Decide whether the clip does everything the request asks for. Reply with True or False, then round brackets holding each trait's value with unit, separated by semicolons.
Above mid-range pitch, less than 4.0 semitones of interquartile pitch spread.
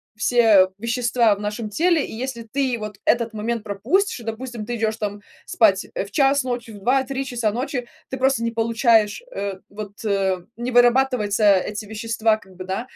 True (230 Hz; 3.0 semitones)